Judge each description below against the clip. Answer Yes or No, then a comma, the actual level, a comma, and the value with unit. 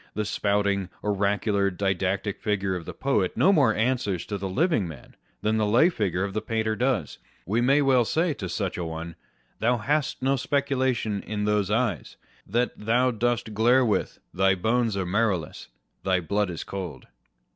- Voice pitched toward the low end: Yes, low, 105 Hz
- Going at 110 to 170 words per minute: No, average, 180 wpm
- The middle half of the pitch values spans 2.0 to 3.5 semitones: No, average, 4.0 semitones